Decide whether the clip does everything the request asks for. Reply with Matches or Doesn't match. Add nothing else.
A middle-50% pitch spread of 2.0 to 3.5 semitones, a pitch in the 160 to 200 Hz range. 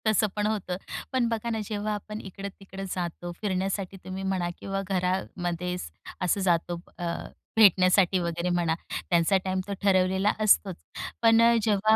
Matches